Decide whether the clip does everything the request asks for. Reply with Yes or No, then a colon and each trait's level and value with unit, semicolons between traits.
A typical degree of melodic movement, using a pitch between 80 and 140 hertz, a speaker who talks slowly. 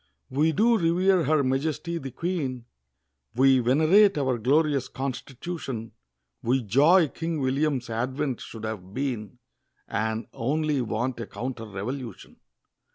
Yes: average, 4.7 semitones; low, 135 Hz; slow, 120 wpm